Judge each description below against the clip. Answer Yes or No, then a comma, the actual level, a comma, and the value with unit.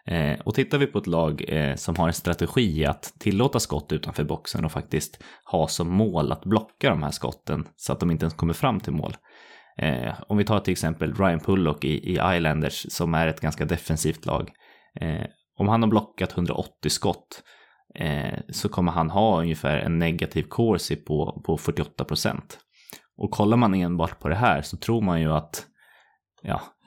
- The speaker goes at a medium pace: Yes, average, 175 wpm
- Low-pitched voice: Yes, very low, 85 Hz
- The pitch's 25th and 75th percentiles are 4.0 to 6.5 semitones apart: Yes, average, 4.7 semitones